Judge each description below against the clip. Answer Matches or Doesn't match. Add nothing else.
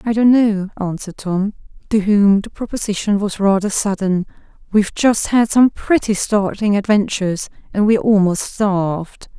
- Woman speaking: Matches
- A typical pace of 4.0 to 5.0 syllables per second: Matches